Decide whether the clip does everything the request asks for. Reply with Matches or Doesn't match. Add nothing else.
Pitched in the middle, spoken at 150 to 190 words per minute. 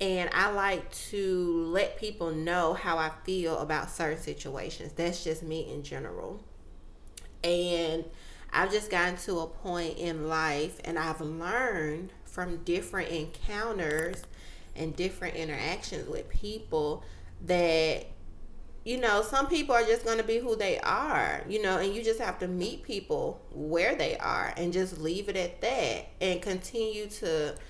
Matches